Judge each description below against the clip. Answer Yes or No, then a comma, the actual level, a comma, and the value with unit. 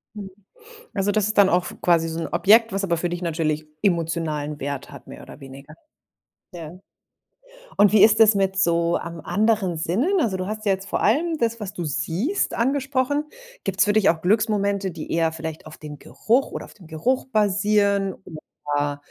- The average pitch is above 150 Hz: Yes, high, 190 Hz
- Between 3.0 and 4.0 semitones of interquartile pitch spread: No, average, 4.7 semitones